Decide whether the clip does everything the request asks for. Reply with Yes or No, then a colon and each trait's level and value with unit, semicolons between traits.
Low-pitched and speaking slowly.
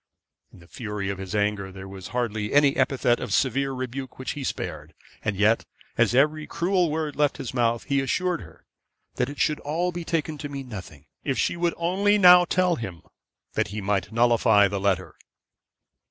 No: low, 125 Hz; average, 190 wpm